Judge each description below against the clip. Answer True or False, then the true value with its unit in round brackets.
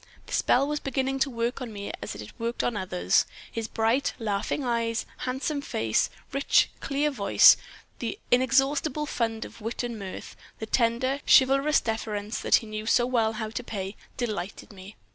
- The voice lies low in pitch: False (230 Hz)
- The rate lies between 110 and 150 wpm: False (170 wpm)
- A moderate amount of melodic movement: True (3.7 semitones)